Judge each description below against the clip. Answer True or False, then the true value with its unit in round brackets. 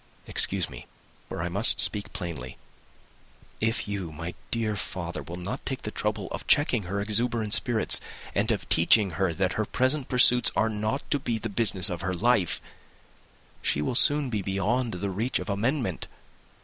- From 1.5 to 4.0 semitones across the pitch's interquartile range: False (4.5 semitones)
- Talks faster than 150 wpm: True (175 wpm)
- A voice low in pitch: True (105 Hz)